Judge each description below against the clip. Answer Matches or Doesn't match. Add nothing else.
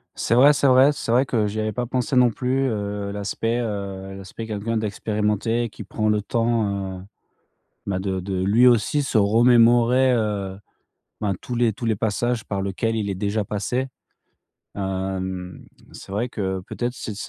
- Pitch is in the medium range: Doesn't match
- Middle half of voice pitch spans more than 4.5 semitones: Doesn't match